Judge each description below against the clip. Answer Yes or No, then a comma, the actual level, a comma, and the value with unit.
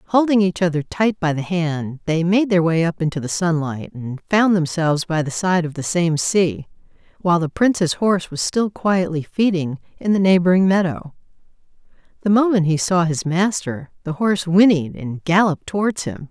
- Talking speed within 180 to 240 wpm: Yes, average, 185 wpm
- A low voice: No, medium, 175 Hz